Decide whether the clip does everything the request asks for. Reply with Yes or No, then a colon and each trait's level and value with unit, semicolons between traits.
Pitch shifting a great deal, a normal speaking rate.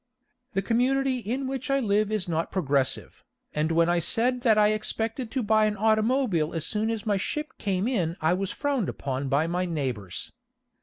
Yes: wide, 6.0 semitones; average, 190 wpm